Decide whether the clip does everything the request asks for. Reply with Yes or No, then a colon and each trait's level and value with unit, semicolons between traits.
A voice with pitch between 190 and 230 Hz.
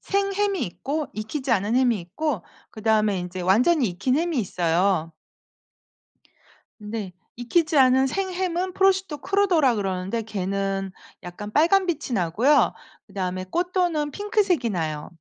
No: high, 245 Hz